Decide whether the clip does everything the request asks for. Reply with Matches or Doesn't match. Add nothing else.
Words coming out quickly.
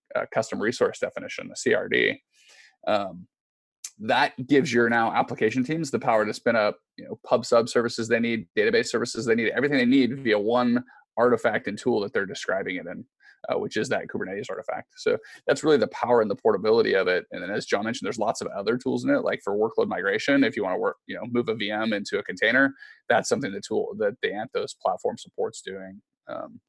Matches